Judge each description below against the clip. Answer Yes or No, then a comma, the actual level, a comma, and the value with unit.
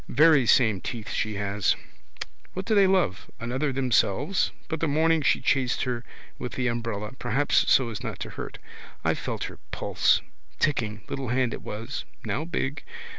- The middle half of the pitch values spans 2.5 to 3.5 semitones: No, average, 4.8 semitones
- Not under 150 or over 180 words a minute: Yes, average, 170 wpm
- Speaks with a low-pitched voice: Yes, low, 130 Hz